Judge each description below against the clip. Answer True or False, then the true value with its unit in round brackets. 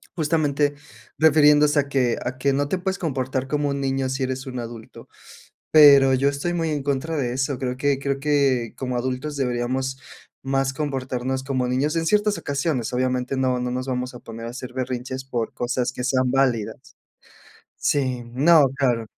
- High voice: False (135 Hz)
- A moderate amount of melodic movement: False (2.2 semitones)